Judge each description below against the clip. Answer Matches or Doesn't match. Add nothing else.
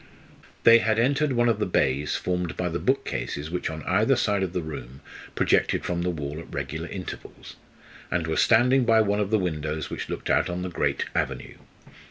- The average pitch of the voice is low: Matches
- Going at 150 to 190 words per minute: Doesn't match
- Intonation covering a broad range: Matches